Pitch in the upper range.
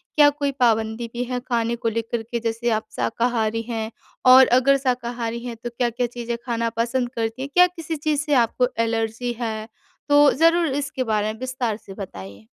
Yes: high, 235 Hz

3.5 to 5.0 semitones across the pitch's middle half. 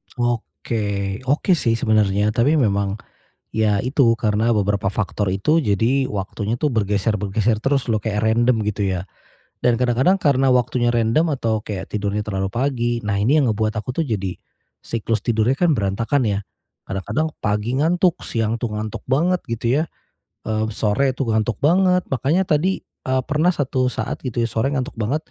Yes: average, 4.4 semitones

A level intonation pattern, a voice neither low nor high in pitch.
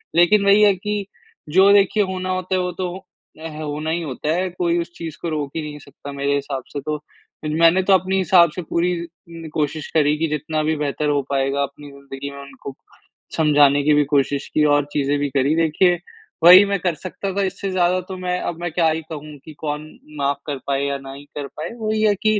No: average, 3.9 semitones; medium, 160 Hz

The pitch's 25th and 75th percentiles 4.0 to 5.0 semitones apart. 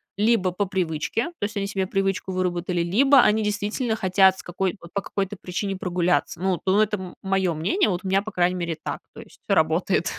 No: narrow, 2.4 semitones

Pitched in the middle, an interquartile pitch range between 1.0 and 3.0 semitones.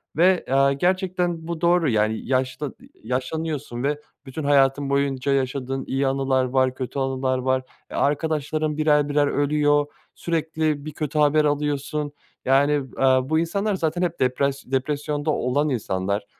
Yes: medium, 145 Hz; narrow, 2.6 semitones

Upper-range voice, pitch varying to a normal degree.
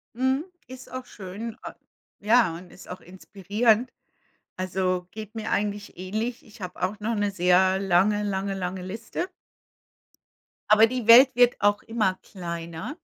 Yes: high, 205 Hz; average, 3.7 semitones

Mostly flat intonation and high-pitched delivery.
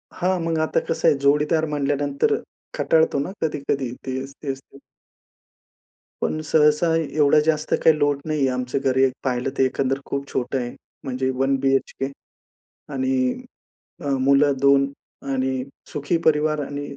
No: narrow, 2.2 semitones; medium, 140 Hz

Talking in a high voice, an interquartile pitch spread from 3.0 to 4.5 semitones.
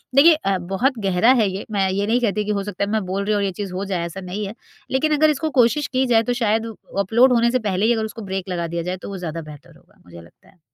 Yes: high, 200 Hz; average, 4.1 semitones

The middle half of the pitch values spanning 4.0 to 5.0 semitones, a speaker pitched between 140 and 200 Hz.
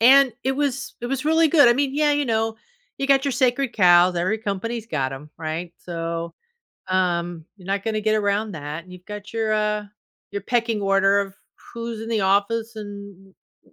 No: average, 4.3 semitones; high, 210 Hz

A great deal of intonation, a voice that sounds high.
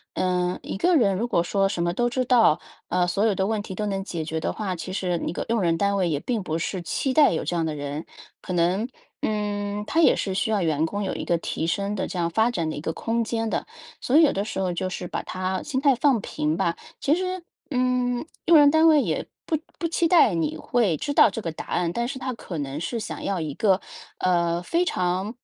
Yes: wide, 5.8 semitones; high, 195 Hz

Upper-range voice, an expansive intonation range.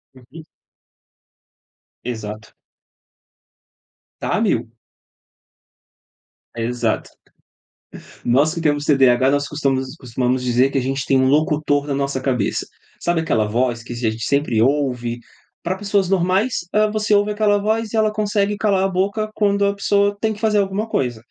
No: medium, 150 Hz; wide, 8.0 semitones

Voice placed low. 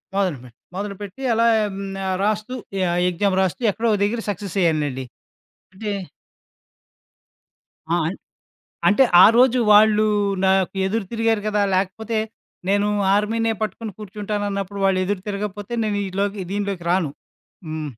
No: high, 205 Hz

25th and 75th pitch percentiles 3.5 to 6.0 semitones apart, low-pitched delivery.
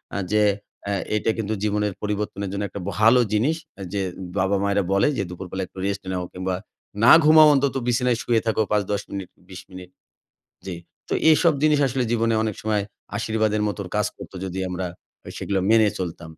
No: average, 2.8 semitones; low, 105 Hz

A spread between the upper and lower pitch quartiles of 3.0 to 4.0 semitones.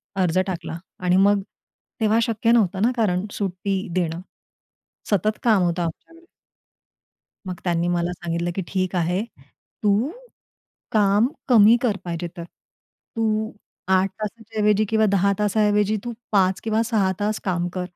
Yes: average, 3.3 semitones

